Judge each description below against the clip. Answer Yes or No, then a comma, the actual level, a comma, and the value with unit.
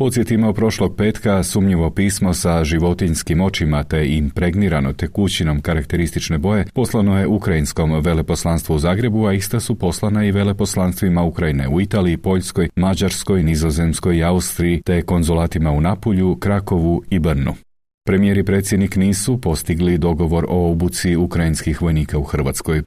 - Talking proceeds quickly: No, average, 135 wpm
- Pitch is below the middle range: Yes, very low, 90 Hz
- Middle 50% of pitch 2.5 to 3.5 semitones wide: Yes, average, 3.1 semitones